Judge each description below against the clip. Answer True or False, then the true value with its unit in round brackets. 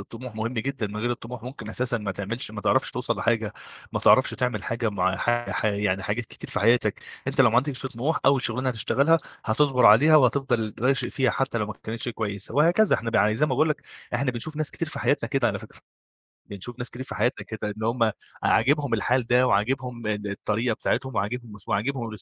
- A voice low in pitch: True (120 Hz)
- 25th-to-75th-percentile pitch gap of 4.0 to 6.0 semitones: False (3.3 semitones)